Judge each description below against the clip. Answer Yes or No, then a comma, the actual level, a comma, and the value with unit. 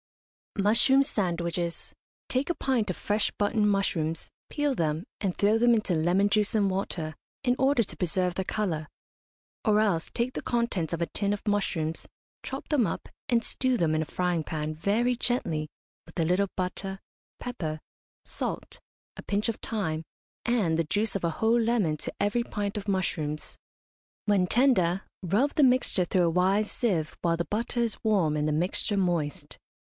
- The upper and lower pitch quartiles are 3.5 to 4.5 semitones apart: No, average, 5.1 semitones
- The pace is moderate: Yes, average, 175 wpm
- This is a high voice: Yes, high, 195 Hz